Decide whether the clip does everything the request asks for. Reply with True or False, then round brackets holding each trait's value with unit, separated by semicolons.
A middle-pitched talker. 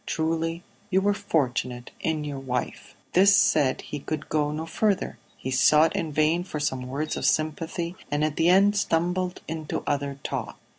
True (155 Hz)